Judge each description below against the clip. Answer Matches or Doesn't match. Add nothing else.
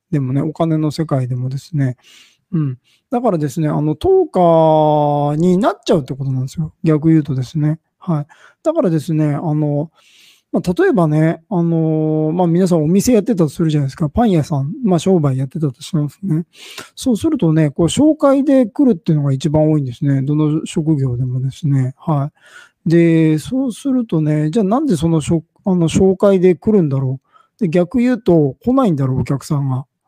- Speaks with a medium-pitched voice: Matches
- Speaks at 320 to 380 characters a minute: Matches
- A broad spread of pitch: Doesn't match